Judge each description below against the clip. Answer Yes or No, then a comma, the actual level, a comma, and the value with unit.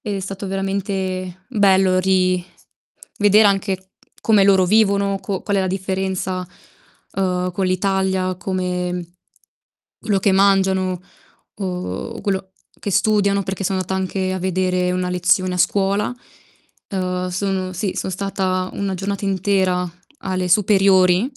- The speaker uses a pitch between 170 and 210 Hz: Yes, high, 190 Hz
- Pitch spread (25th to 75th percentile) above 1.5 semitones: No, narrow, 1.2 semitones